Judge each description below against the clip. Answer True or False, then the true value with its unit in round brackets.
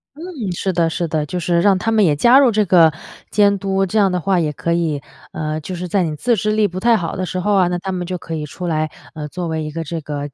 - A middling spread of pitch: True (3.5 semitones)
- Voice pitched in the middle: True (175 Hz)